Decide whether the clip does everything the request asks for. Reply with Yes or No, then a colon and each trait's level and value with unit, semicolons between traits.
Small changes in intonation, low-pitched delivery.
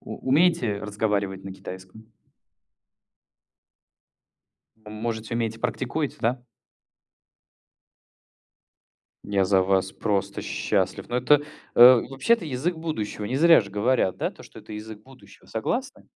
No: average, 4.5 semitones; low, 110 Hz